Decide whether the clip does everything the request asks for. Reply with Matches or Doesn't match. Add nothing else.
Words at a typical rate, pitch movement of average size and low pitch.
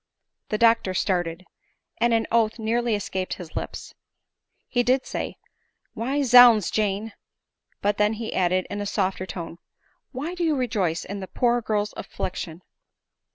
Doesn't match